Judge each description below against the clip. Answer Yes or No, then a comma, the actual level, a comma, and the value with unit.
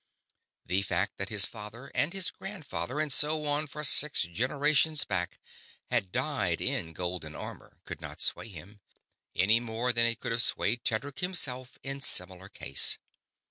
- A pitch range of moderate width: No, wide, 6.9 semitones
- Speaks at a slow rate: No, average, 160 wpm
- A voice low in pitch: Yes, low, 115 Hz